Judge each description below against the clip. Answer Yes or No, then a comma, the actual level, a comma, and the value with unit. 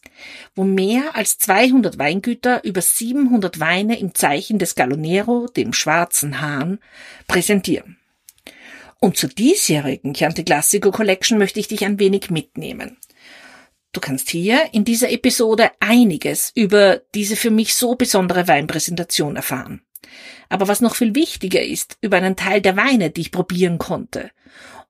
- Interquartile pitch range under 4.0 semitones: No, average, 4.9 semitones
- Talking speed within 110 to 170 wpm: Yes, average, 140 wpm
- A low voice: No, high, 205 Hz